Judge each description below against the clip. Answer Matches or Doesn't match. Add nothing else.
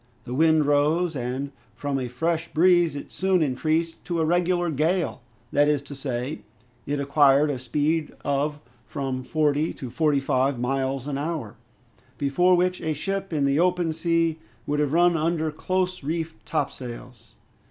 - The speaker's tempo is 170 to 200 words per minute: Doesn't match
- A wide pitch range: Doesn't match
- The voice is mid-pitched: Matches